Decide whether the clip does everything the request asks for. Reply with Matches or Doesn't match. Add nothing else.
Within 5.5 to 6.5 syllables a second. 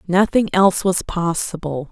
Doesn't match